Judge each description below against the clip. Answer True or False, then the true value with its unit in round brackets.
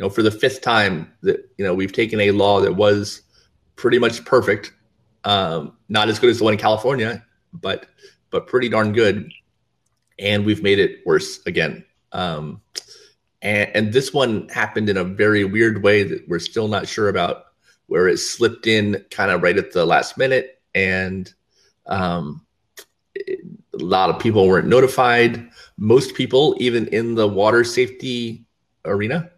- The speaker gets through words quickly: False (170 wpm)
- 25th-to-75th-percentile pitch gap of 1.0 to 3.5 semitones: False (4.2 semitones)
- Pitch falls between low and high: False (110 Hz)